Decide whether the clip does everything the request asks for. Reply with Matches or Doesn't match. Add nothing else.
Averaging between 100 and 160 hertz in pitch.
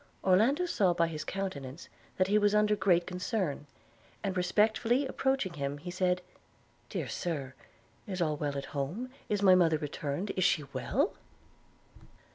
Doesn't match